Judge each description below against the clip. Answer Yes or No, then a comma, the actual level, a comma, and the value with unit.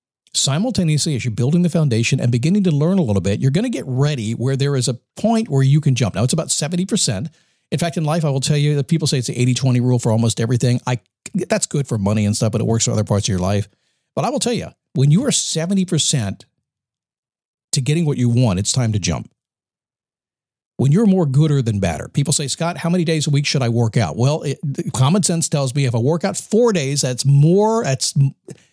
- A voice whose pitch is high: No, medium, 140 Hz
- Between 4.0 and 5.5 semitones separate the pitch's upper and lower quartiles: Yes, average, 5.2 semitones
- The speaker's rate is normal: No, fast, 245 wpm